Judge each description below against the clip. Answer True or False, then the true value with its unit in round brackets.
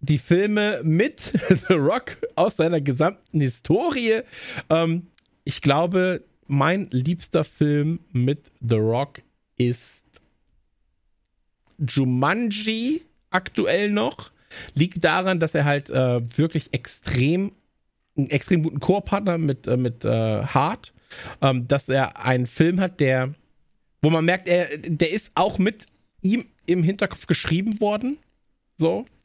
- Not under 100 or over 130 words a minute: True (125 wpm)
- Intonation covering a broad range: True (5.7 semitones)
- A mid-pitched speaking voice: True (160 Hz)